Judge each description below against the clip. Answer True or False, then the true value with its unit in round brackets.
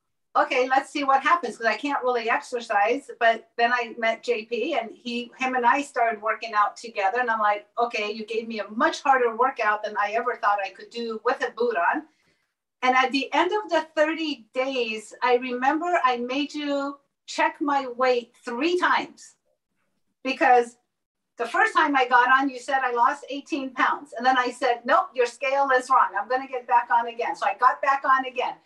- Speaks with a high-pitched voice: True (250 Hz)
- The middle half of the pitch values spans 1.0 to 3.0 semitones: True (2.7 semitones)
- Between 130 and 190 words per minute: False (205 wpm)